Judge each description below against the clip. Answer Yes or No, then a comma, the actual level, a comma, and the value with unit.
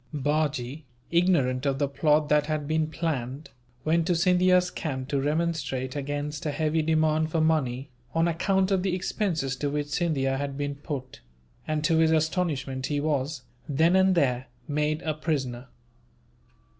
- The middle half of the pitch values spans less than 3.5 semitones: Yes, average, 2.8 semitones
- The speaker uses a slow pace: No, average, 155 wpm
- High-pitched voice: No, medium, 150 Hz